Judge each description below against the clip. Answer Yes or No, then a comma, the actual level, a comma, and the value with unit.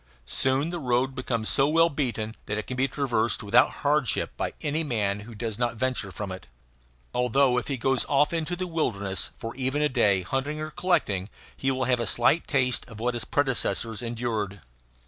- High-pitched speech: No, low, 125 Hz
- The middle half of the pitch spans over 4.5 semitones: No, average, 4.2 semitones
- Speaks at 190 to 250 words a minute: Yes, average, 195 wpm